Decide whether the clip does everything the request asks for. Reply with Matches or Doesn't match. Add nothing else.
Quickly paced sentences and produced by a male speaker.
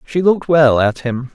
Matches